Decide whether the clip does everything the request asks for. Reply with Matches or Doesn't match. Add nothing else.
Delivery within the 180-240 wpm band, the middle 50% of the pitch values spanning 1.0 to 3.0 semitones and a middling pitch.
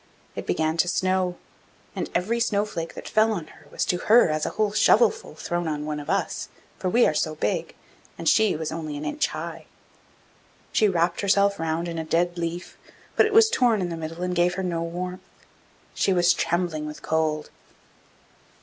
Doesn't match